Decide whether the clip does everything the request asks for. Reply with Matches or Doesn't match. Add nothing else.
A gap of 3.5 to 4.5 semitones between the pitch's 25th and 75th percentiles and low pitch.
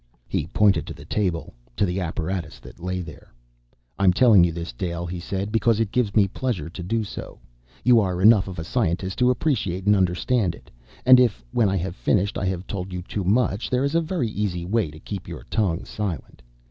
Matches